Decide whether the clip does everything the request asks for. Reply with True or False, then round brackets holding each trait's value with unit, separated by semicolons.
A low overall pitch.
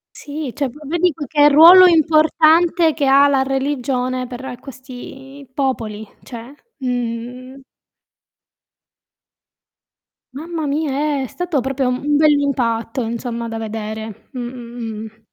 False (265 Hz)